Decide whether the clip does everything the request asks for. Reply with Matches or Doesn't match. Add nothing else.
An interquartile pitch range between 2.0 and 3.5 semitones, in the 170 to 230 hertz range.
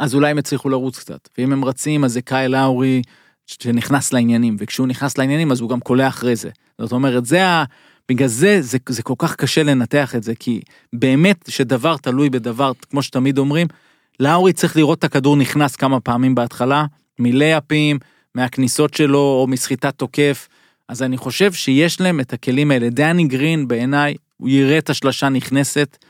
Doesn't match